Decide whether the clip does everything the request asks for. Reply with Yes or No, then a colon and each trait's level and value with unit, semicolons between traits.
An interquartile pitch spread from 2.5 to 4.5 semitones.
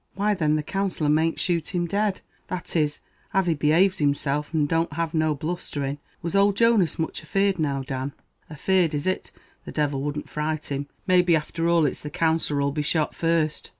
Yes: average, 3.2 semitones